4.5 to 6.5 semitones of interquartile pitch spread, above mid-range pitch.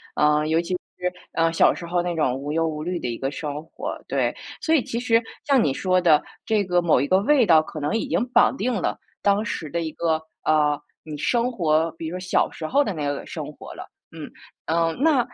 No: average, 4.8 semitones; medium, 165 Hz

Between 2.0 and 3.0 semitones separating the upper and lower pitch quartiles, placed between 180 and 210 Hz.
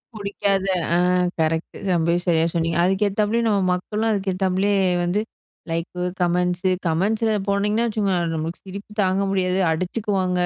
Yes: average, 2.7 semitones; high, 190 Hz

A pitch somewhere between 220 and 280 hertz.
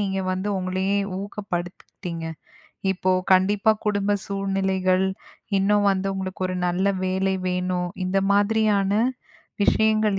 No: high, 195 Hz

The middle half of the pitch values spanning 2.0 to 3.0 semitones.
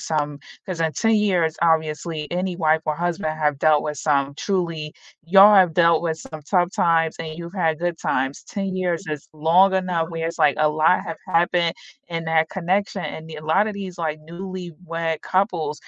Yes: narrow, 2.5 semitones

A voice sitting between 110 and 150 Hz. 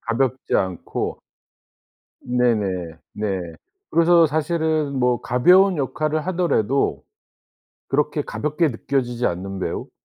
Yes: low, 135 Hz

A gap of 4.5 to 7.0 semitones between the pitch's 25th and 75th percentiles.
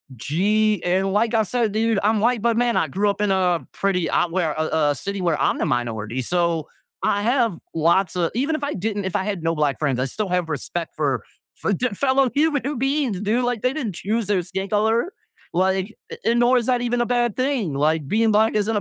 Yes: wide, 5.6 semitones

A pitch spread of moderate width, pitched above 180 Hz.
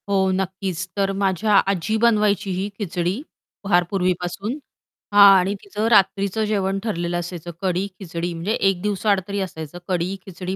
No: narrow, 2.2 semitones; high, 190 Hz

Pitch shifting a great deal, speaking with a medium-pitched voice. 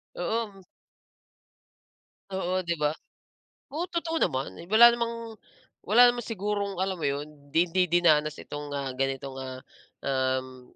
Yes: wide, 7.7 semitones; medium, 175 Hz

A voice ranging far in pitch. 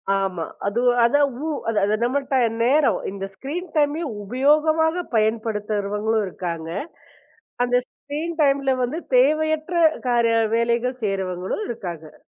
Yes: wide, 5.8 semitones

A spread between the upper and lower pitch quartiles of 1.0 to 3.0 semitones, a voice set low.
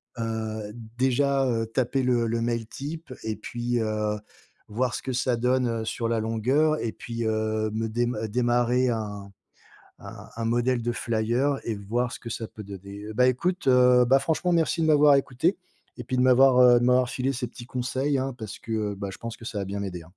Yes: narrow, 2.6 semitones; low, 120 Hz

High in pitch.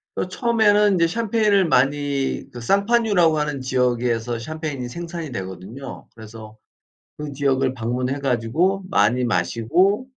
No: medium, 140 Hz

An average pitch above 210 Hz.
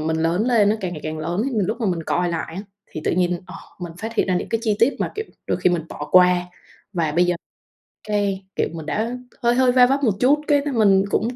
No: high, 195 Hz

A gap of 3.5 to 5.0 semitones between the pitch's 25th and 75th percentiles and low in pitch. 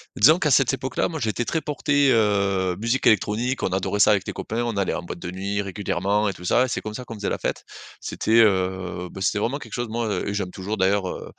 Yes: average, 3.9 semitones; low, 105 Hz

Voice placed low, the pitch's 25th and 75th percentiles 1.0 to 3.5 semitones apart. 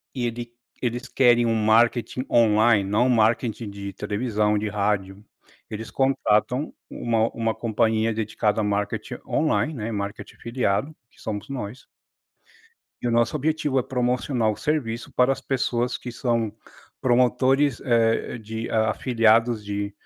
Yes: low, 115 Hz; average, 2.7 semitones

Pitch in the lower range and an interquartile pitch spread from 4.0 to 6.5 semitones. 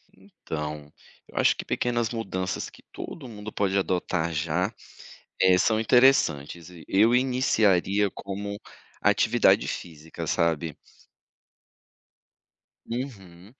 Yes: very low, 95 Hz; average, 4.9 semitones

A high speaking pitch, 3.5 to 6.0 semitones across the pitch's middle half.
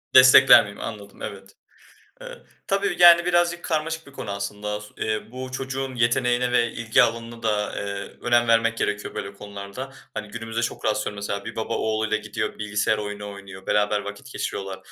No: low, 110 Hz; average, 3.8 semitones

